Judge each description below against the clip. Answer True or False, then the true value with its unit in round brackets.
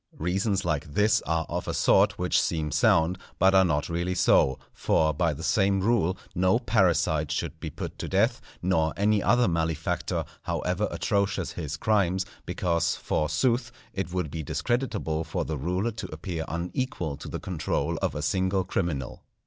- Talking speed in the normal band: True (165 wpm)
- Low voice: True (90 Hz)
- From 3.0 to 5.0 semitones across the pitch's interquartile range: True (3.6 semitones)